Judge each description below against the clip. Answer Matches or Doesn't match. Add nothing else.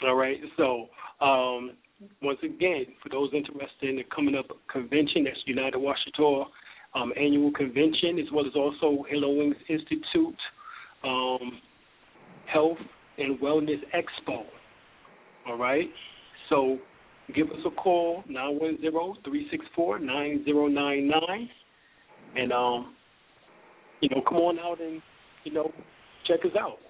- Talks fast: Doesn't match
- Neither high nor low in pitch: Matches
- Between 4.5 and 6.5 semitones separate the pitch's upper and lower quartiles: Doesn't match